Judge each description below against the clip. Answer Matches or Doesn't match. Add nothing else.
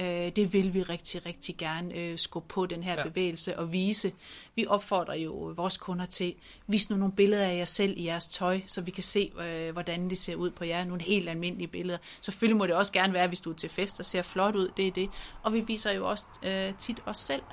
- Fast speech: Matches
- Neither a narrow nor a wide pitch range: Doesn't match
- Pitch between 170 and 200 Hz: Matches